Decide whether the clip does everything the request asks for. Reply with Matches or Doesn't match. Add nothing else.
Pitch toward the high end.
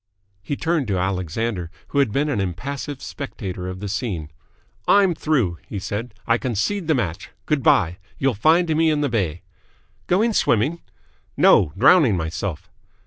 Doesn't match